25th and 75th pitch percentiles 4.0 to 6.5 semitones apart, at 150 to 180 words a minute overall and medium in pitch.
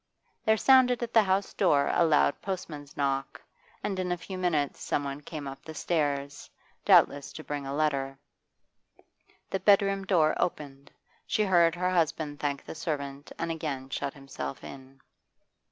Yes: average, 4.5 semitones; average, 155 wpm; medium, 155 Hz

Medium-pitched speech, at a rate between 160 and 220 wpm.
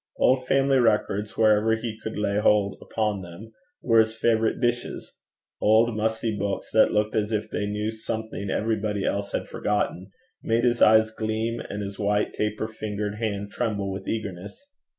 No: low, 110 Hz; average, 165 wpm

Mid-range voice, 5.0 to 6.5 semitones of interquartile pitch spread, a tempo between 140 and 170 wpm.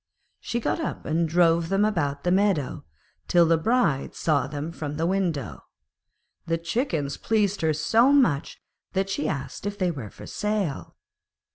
Yes: medium, 170 Hz; average, 5.3 semitones; average, 160 wpm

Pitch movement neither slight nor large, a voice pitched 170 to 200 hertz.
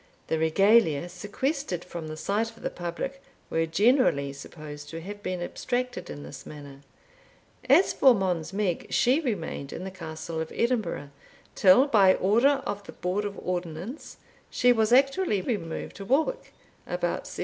No: wide, 7.0 semitones; high, 190 Hz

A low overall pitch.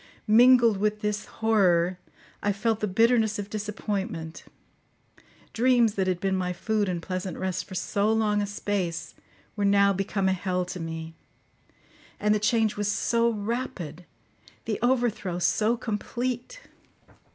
No: high, 205 Hz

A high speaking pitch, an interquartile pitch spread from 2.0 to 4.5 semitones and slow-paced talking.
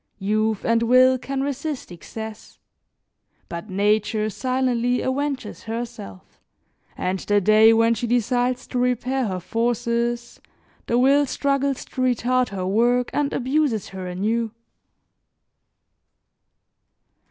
Yes: high, 235 Hz; average, 3.0 semitones; slow, 110 wpm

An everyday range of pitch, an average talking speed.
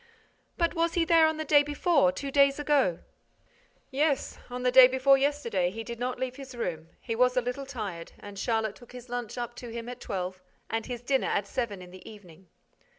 No: average, 4.2 semitones; fast, 215 wpm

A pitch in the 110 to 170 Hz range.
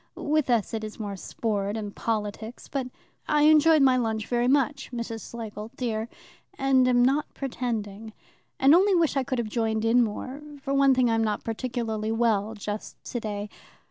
No: high, 235 Hz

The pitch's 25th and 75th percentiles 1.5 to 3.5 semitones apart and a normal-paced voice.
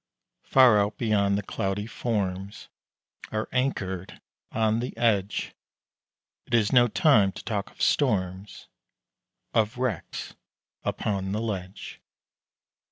No: average, 3.1 semitones; slow, 110 wpm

